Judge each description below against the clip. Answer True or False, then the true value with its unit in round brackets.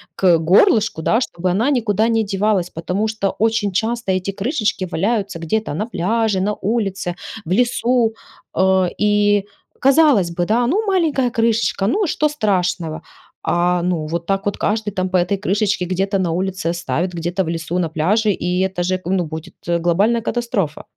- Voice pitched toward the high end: True (195 Hz)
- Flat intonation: False (4.0 semitones)